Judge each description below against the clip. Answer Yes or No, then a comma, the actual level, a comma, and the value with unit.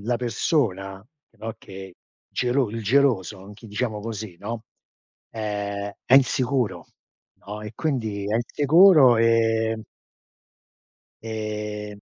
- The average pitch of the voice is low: Yes, low, 110 Hz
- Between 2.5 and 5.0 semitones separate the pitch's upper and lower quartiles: Yes, average, 2.8 semitones